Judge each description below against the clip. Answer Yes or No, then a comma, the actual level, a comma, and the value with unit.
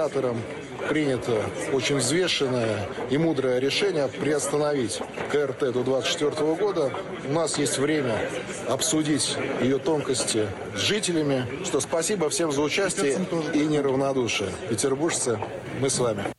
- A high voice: No, medium, 140 Hz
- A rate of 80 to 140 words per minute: Yes, average, 115 wpm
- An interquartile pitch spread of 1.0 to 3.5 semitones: Yes, average, 3.2 semitones